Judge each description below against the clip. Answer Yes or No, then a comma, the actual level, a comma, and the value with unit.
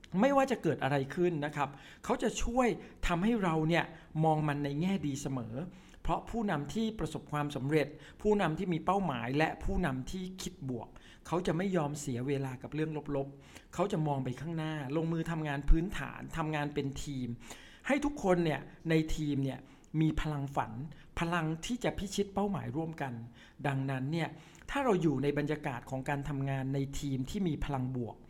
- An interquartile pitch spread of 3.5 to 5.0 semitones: Yes, average, 4.1 semitones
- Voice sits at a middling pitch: Yes, medium, 155 Hz